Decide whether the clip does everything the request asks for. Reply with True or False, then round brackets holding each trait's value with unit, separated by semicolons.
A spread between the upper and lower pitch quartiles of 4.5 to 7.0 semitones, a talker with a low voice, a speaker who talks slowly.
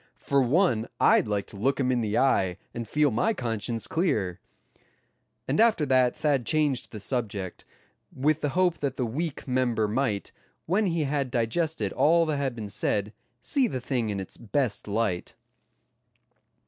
False (5.4 semitones; 125 Hz; 165 wpm)